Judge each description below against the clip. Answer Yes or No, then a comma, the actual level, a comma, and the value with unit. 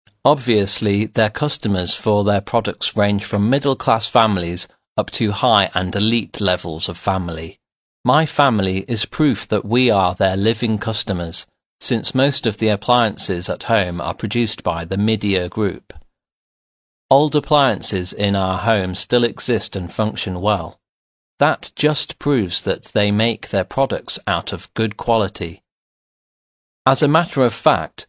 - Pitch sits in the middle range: No, low, 105 Hz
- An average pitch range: Yes, average, 4.0 semitones